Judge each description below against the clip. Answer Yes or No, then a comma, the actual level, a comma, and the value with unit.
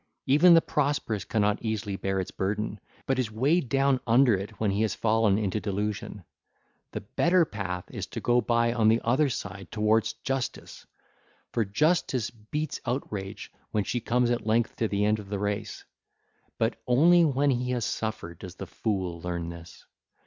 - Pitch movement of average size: Yes, average, 3.8 semitones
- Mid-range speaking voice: No, low, 110 Hz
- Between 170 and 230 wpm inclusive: Yes, average, 175 wpm